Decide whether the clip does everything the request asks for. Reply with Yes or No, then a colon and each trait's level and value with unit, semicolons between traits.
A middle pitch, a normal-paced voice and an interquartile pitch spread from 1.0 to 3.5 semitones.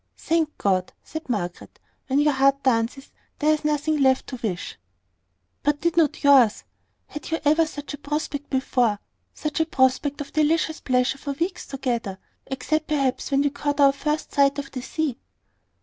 No: very high, 280 Hz; average, 170 wpm; narrow, 2.5 semitones